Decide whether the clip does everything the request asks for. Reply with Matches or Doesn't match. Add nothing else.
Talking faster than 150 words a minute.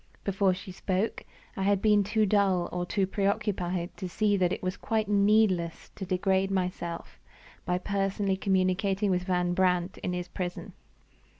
Matches